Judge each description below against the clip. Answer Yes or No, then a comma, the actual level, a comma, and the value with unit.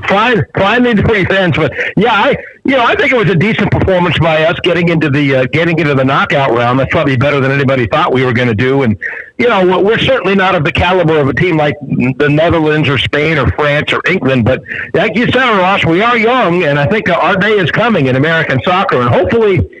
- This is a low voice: No, medium, 155 Hz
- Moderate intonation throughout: Yes, average, 4.8 semitones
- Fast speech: Yes, fast, 235 wpm